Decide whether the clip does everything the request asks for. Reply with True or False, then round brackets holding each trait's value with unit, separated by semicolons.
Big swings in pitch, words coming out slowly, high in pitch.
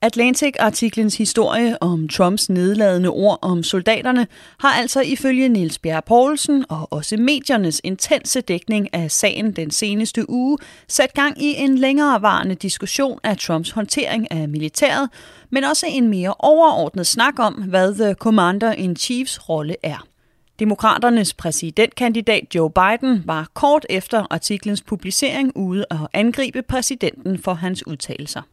True (5.8 semitones; 135 wpm; 220 Hz)